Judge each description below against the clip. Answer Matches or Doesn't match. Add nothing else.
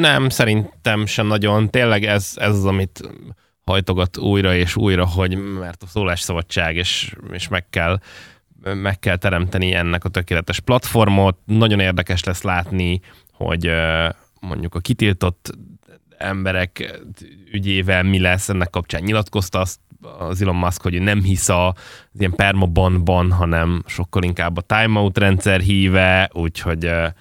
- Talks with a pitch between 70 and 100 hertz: Matches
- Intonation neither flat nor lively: Doesn't match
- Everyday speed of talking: Matches